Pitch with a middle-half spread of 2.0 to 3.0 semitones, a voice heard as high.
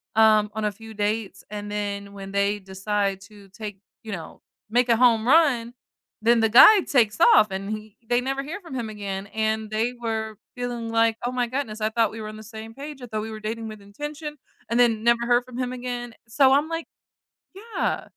Yes: average, 2.7 semitones; high, 225 Hz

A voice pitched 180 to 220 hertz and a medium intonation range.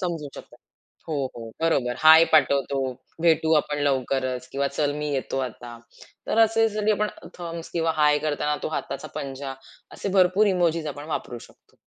No: medium, 150 Hz; average, 3.5 semitones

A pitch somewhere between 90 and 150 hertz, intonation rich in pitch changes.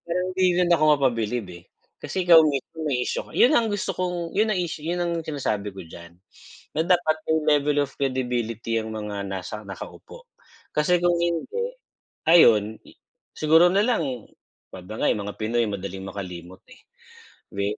Yes: medium, 140 Hz; wide, 8.5 semitones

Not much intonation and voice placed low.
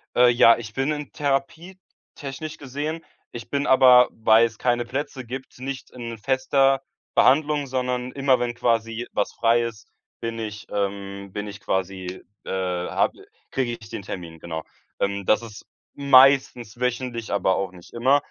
No: average, 4.2 semitones; low, 120 Hz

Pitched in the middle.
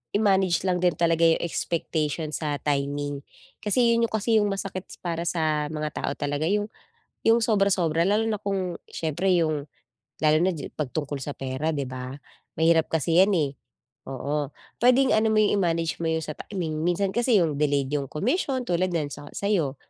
Yes: medium, 165 Hz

